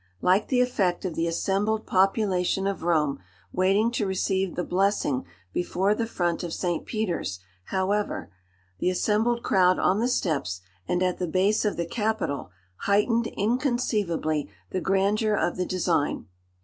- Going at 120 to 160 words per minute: Yes, average, 150 wpm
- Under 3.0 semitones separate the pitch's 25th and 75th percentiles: No, average, 3.3 semitones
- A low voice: No, high, 190 Hz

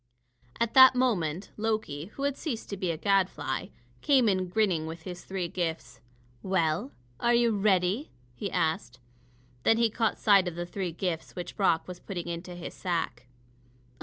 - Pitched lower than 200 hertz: Yes, medium, 185 Hz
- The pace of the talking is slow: No, average, 165 wpm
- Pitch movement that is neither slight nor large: Yes, average, 4.4 semitones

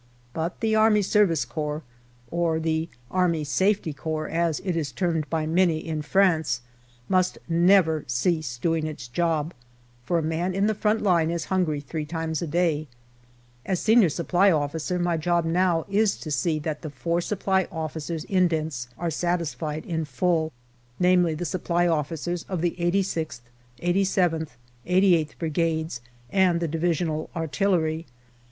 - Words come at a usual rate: Yes, average, 145 wpm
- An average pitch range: No, narrow, 2.3 semitones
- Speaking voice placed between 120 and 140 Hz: No, medium, 165 Hz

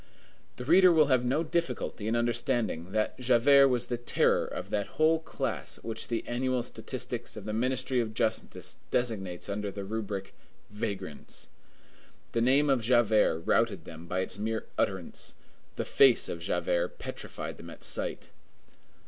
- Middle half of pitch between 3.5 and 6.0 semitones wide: Yes, average, 3.9 semitones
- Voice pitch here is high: No, low, 120 Hz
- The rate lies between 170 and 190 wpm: No, average, 155 wpm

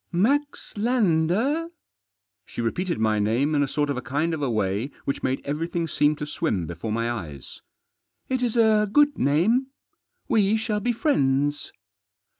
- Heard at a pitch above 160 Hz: No, medium, 150 Hz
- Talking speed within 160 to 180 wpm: Yes, average, 175 wpm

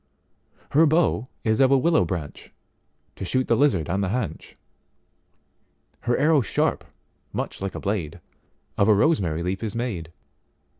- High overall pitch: No, low, 100 Hz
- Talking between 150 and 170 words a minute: No, slow, 135 wpm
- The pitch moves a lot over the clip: Yes, wide, 7.4 semitones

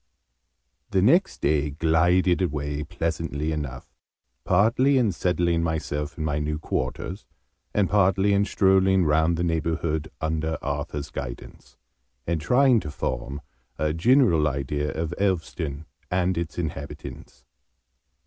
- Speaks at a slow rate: Yes, slow, 120 wpm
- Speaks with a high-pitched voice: No, very low, 80 Hz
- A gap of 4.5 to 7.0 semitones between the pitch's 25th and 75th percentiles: No, average, 3.6 semitones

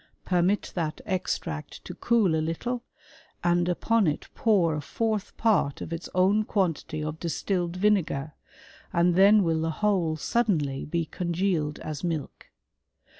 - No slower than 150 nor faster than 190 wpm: No, average, 140 wpm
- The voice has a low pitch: No, medium, 175 Hz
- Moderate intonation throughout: Yes, average, 4.0 semitones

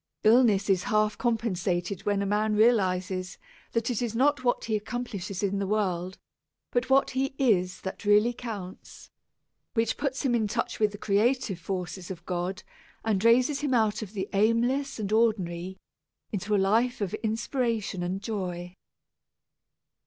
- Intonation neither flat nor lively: Yes, average, 3.8 semitones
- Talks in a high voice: Yes, high, 210 Hz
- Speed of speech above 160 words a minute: No, average, 155 wpm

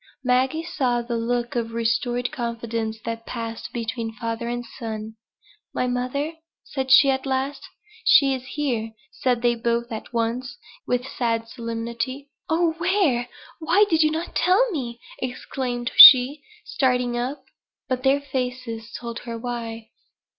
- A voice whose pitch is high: Yes, high, 245 Hz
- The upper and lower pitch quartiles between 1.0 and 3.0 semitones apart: Yes, narrow, 2.4 semitones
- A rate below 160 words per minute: Yes, average, 140 wpm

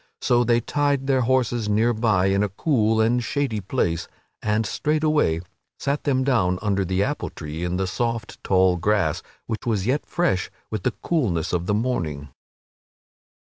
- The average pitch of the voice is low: Yes, low, 110 Hz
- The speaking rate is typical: Yes, average, 165 wpm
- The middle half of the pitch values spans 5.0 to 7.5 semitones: Yes, wide, 5.4 semitones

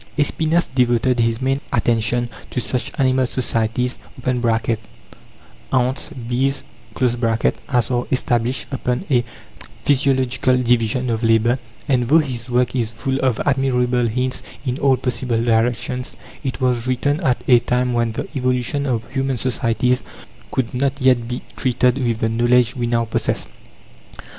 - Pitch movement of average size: No, narrow, 1.7 semitones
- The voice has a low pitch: Yes, low, 125 Hz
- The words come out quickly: No, average, 140 wpm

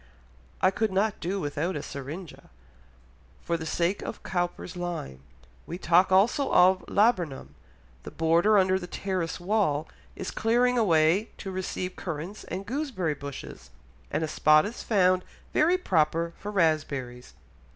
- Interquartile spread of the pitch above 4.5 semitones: No, average, 3.9 semitones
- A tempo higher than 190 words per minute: No, average, 145 wpm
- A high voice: No, medium, 180 Hz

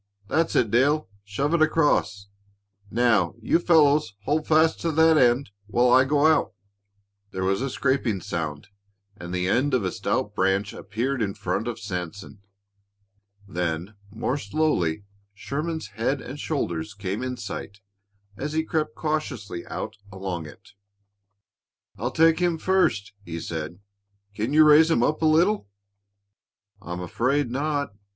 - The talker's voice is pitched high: No, low, 120 Hz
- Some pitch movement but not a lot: No, wide, 7.5 semitones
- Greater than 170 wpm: No, average, 145 wpm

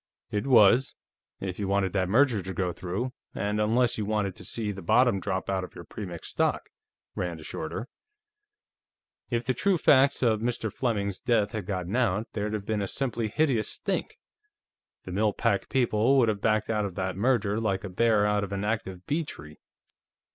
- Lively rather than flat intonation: No, average, 3.4 semitones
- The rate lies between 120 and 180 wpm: No, average, 190 wpm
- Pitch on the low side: Yes, low, 105 Hz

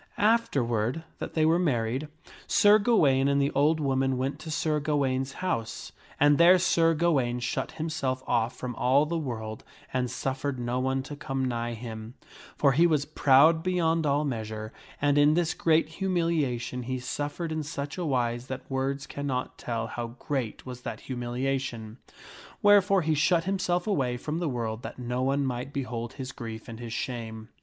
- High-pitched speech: No, low, 135 Hz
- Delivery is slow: No, average, 175 wpm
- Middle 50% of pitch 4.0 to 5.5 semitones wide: Yes, average, 4.3 semitones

